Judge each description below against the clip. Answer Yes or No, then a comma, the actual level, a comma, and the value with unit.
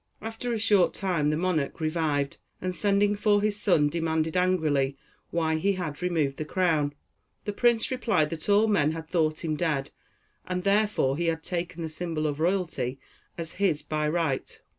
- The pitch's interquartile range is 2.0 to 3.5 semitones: No, average, 4.2 semitones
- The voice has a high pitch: No, medium, 165 Hz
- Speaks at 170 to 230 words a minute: Yes, average, 175 wpm